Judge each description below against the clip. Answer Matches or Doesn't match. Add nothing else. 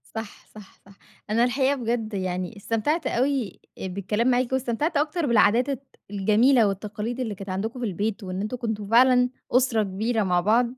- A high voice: Matches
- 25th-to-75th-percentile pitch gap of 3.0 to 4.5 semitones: Matches